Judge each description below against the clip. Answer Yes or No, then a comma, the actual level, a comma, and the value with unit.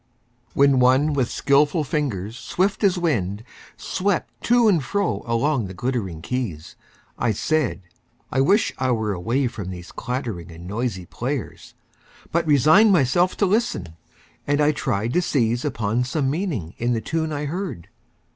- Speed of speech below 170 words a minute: Yes, average, 155 wpm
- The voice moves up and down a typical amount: No, wide, 6.2 semitones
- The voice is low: Yes, low, 130 Hz